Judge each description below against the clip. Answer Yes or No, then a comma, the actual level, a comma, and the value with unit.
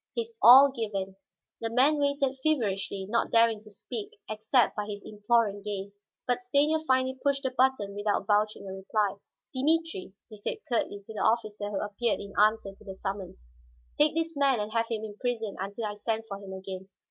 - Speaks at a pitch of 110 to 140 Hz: No, high, 220 Hz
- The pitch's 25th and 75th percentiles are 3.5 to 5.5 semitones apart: Yes, average, 4.3 semitones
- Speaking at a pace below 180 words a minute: No, average, 185 wpm